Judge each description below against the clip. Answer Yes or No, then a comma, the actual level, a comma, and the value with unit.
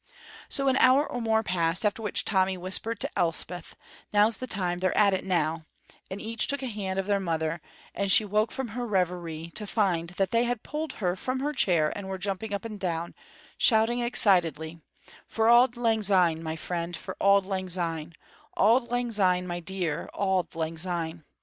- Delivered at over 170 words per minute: Yes, average, 195 wpm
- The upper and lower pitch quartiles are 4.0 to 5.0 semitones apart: Yes, average, 4.4 semitones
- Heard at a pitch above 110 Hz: Yes, high, 190 Hz